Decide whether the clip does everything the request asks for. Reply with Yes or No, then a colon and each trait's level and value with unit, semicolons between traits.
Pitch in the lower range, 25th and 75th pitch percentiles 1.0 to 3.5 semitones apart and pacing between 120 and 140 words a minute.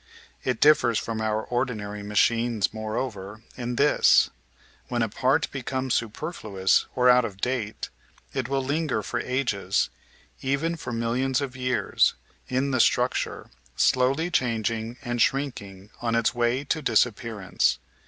Yes: low, 120 Hz; average, 3.2 semitones; slow, 135 wpm